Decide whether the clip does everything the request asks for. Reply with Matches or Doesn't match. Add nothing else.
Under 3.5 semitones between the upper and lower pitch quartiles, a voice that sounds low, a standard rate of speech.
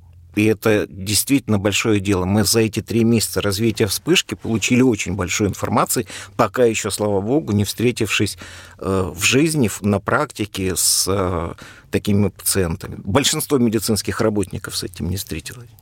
Matches